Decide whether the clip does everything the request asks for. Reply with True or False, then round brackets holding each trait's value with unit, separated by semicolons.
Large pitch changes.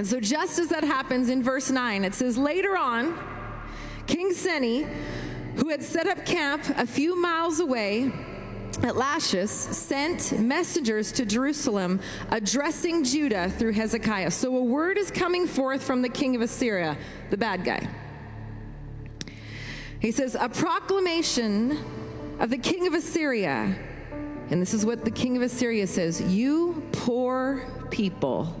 True (6.0 semitones)